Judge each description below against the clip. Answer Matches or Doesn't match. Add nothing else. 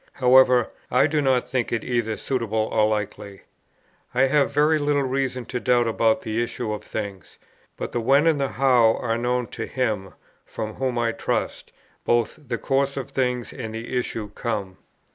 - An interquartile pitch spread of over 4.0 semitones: Doesn't match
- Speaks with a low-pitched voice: Matches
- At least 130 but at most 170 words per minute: Doesn't match